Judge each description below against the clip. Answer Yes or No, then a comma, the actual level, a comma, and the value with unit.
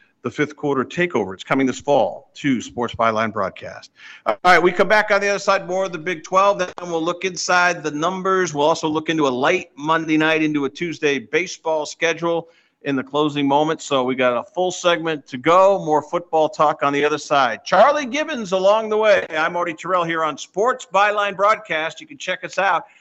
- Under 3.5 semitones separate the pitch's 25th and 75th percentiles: No, average, 4.1 semitones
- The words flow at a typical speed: No, fast, 210 wpm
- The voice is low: No, medium, 165 Hz